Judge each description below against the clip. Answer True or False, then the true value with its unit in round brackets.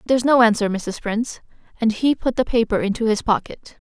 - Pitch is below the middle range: False (230 Hz)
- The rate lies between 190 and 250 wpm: True (200 wpm)